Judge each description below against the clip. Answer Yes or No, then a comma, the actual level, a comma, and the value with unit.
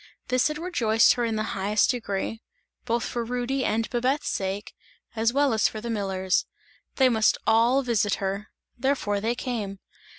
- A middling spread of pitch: Yes, average, 3.2 semitones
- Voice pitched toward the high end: Yes, high, 230 Hz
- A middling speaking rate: Yes, average, 165 wpm